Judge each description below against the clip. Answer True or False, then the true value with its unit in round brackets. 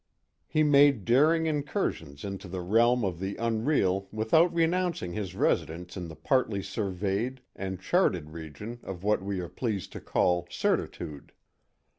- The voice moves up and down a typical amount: False (6.4 semitones)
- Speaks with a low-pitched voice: True (100 Hz)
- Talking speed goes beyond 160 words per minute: False (145 wpm)